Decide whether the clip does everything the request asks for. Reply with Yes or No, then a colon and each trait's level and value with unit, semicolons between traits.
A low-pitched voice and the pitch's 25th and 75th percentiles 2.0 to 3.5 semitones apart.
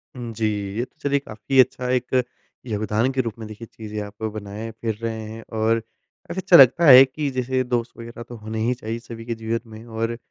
Yes: low, 115 Hz; narrow, 2.4 semitones